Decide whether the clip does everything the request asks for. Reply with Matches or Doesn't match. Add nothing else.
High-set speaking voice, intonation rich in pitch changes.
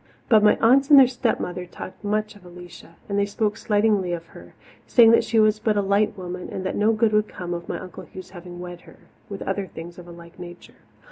Doesn't match